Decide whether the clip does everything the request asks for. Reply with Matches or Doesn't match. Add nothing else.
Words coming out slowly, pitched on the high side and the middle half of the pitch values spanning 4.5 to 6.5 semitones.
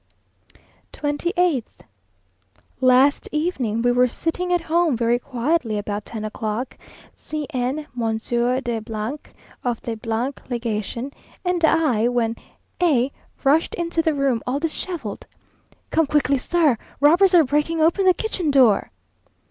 Matches